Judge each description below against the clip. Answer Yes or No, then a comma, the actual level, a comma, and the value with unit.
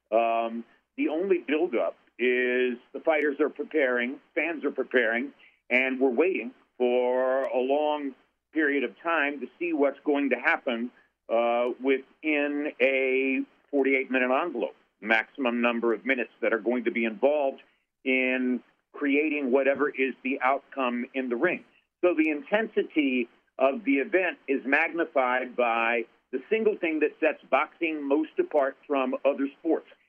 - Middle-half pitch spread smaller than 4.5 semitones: Yes, average, 3.1 semitones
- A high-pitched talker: No, low, 135 Hz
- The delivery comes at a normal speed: Yes, average, 145 wpm